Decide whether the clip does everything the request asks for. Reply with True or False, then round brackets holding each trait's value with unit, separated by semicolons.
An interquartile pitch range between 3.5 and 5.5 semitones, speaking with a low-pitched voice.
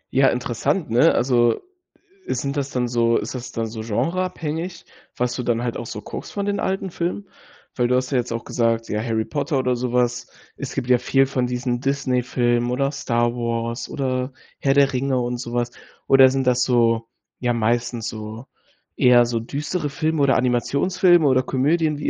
False (2.7 semitones; 125 Hz)